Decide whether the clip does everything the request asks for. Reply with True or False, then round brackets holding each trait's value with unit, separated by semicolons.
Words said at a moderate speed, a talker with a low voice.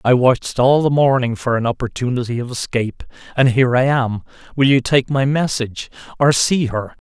True (180 wpm; 125 Hz)